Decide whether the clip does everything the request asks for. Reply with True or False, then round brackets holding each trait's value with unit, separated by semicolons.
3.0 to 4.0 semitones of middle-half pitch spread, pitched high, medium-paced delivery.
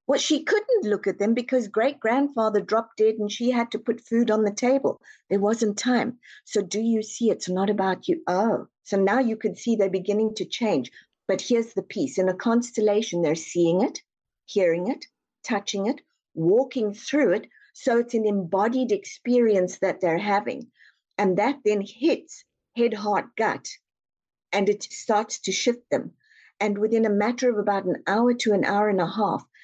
True (3.4 semitones; 220 Hz; 190 wpm)